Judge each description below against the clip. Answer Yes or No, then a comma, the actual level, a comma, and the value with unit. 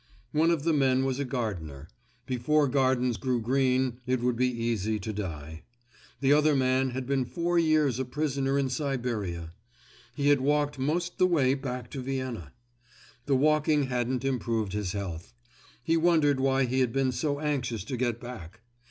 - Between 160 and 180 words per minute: Yes, average, 170 wpm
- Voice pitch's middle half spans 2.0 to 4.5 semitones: Yes, average, 3.3 semitones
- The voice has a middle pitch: No, low, 130 Hz